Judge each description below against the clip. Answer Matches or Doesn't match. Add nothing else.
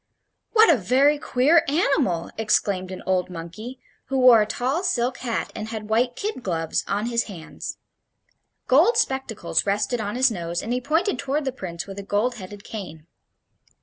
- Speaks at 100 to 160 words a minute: Doesn't match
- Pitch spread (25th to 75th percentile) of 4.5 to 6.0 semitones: Matches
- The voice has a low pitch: Doesn't match